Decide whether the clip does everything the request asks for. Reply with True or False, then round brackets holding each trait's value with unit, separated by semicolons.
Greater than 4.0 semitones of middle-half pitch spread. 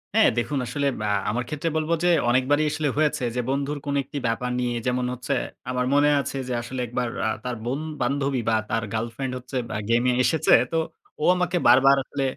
False (2.8 semitones)